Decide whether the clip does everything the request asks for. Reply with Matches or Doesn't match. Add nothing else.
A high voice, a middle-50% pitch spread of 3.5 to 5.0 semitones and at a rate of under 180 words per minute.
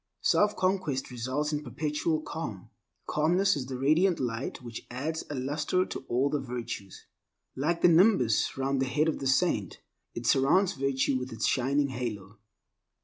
Doesn't match